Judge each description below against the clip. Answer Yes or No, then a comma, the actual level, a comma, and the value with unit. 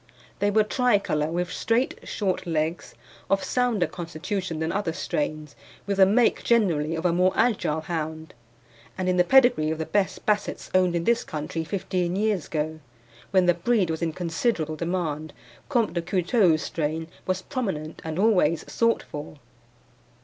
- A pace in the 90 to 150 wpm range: No, average, 160 wpm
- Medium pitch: Yes, medium, 180 Hz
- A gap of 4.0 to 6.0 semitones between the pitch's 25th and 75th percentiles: Yes, average, 4.3 semitones